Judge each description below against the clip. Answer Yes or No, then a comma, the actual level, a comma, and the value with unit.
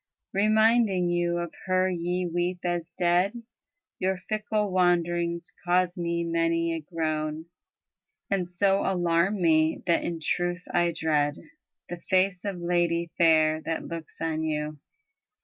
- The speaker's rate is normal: No, slow, 130 wpm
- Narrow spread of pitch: Yes, narrow, 1.7 semitones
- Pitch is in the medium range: Yes, medium, 175 Hz